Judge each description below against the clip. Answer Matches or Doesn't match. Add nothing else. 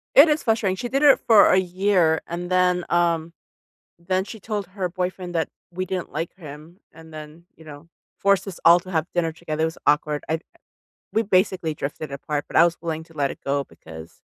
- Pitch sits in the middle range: Matches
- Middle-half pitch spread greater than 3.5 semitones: Doesn't match